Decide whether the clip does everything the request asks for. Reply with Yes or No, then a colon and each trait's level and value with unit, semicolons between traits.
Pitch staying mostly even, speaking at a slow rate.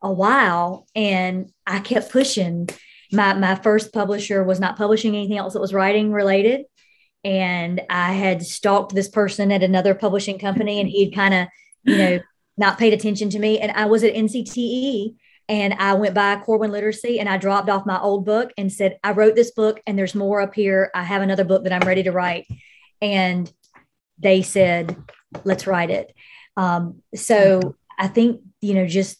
No: narrow, 2.0 semitones; average, 185 wpm